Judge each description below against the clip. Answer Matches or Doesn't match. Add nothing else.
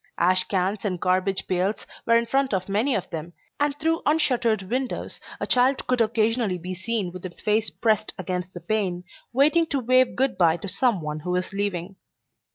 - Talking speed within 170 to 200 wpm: Matches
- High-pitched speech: Matches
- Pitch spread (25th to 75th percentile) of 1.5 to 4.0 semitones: Doesn't match